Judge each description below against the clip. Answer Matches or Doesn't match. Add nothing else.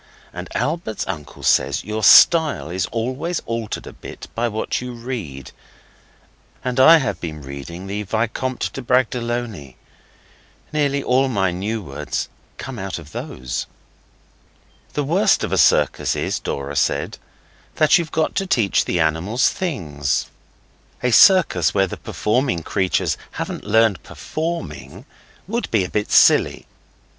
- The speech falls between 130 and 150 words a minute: Matches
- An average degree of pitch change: Doesn't match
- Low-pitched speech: Matches